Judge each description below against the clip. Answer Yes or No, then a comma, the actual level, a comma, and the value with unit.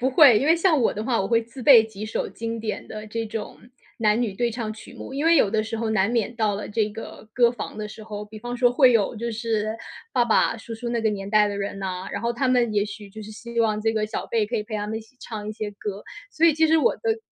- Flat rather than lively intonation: Yes, narrow, 2.2 semitones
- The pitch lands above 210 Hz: Yes, high, 225 Hz